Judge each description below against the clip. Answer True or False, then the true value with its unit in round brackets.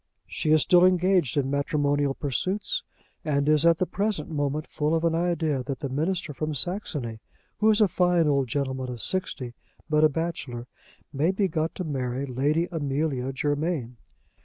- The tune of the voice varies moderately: True (3.8 semitones)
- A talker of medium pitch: True (150 Hz)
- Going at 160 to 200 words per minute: True (170 wpm)